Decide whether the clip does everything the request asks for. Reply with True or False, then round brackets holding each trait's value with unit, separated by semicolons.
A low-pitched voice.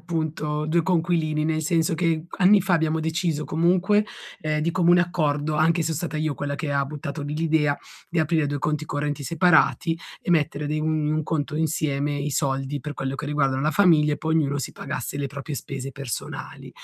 False (155 Hz)